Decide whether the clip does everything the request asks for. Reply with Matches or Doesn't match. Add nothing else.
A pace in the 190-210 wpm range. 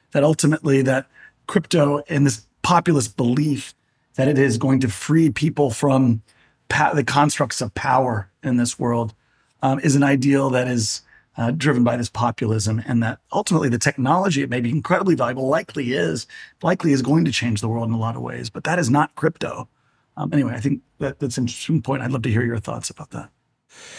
Matches